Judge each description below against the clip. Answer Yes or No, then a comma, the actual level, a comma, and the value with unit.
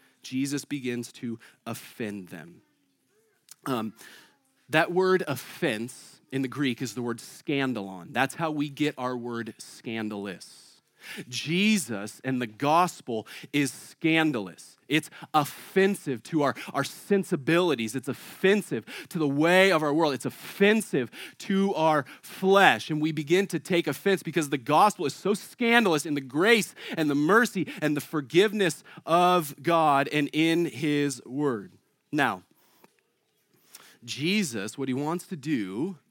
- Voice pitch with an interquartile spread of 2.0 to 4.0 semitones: No, average, 5.0 semitones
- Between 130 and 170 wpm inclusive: Yes, slow, 135 wpm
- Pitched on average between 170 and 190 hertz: No, medium, 150 Hz